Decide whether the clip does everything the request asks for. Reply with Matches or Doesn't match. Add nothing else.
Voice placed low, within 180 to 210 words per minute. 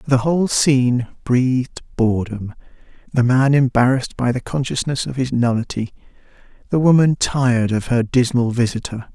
Doesn't match